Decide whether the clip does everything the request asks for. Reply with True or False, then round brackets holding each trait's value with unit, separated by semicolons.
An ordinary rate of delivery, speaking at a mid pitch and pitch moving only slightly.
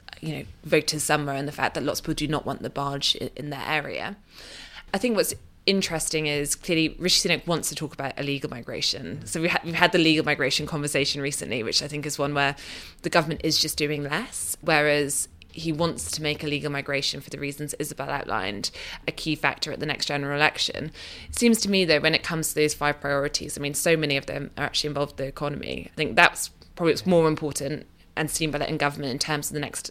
False (235 wpm; 150 Hz; 2.0 semitones)